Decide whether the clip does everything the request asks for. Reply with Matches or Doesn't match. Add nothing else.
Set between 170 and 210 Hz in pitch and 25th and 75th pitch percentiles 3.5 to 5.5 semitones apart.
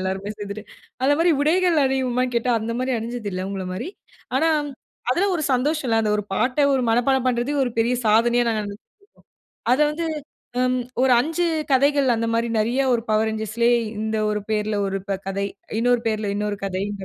Doesn't match